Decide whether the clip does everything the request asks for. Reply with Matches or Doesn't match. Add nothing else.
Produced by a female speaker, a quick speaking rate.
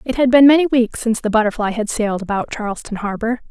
Matches